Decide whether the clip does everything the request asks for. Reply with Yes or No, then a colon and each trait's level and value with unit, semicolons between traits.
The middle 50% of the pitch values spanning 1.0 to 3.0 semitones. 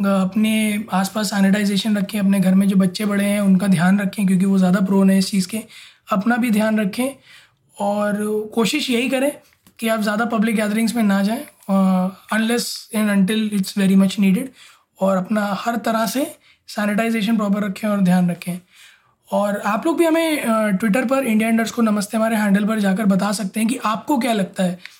Yes: narrow, 2.4 semitones